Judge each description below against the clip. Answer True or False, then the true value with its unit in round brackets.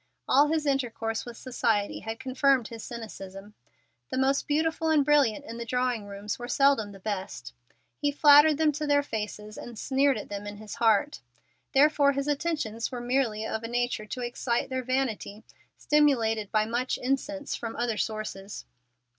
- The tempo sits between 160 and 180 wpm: True (170 wpm)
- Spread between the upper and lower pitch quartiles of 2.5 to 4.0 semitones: False (4.5 semitones)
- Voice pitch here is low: False (245 Hz)